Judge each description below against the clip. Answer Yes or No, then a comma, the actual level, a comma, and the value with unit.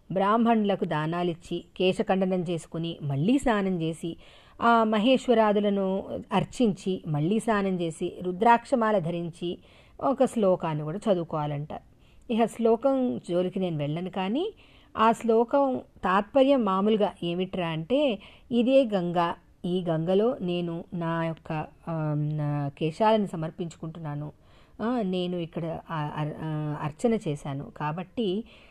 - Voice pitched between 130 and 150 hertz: No, medium, 185 Hz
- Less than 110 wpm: Yes, average, 95 wpm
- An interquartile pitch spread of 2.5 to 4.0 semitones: No, average, 5.1 semitones